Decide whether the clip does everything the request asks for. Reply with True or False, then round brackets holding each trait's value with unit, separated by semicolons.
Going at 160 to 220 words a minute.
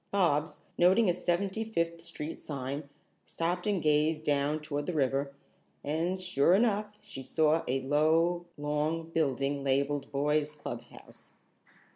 False (135 wpm)